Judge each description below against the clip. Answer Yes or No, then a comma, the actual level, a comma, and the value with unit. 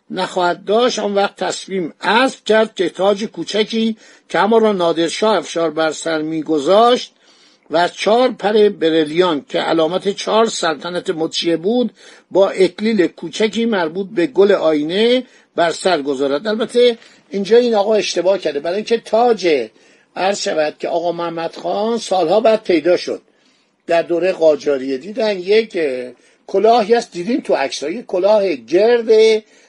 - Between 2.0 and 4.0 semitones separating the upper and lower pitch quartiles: No, average, 4.8 semitones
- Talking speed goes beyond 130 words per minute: Yes, average, 140 wpm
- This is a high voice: Yes, high, 195 Hz